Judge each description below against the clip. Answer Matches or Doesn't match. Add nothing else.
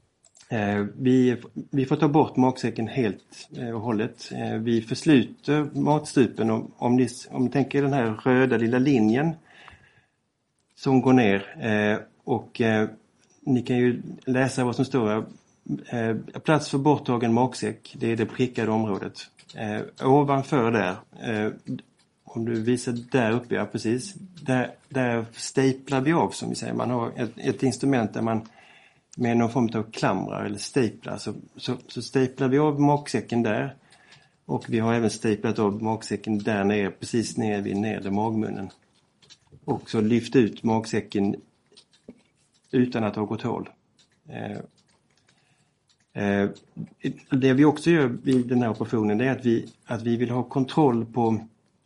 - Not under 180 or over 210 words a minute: Doesn't match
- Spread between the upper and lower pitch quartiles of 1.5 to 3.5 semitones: Matches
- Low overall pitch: Matches